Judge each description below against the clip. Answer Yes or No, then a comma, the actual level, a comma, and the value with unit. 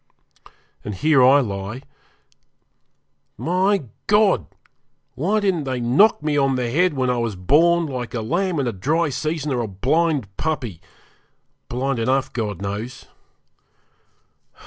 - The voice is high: No, low, 135 Hz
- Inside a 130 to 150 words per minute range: Yes, slow, 135 wpm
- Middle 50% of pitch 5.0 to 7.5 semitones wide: Yes, wide, 5.6 semitones